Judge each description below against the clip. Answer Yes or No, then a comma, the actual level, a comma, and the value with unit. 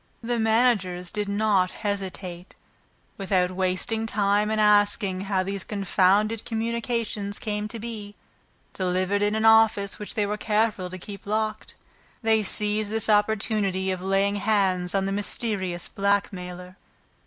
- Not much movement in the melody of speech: Yes, narrow, 2.3 semitones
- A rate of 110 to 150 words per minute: Yes, slow, 135 wpm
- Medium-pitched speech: No, high, 205 Hz